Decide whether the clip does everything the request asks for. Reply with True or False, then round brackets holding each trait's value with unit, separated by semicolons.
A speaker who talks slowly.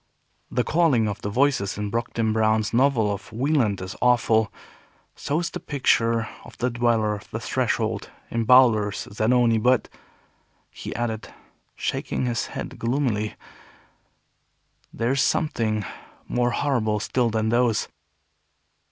True (130 wpm)